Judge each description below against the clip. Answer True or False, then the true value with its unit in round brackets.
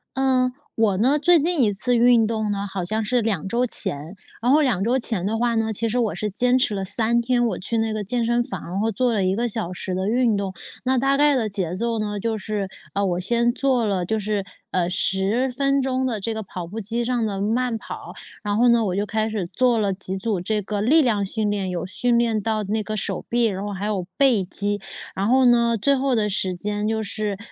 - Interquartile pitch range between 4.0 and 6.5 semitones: False (3.3 semitones)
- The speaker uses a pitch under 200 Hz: False (220 Hz)